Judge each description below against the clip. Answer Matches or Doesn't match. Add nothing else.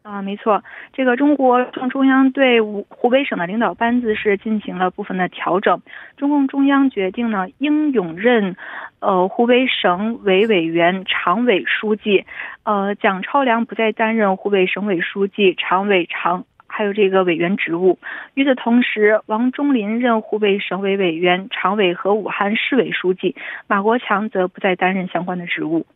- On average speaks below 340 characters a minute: Matches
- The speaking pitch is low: Doesn't match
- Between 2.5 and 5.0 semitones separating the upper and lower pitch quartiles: Matches